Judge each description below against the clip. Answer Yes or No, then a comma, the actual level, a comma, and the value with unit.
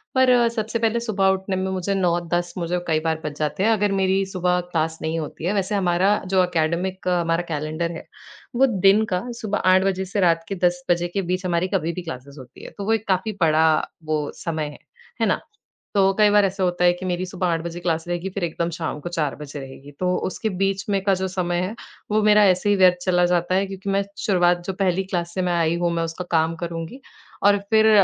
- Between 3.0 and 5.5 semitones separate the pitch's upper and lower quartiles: No, narrow, 2.6 semitones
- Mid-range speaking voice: Yes, medium, 180 Hz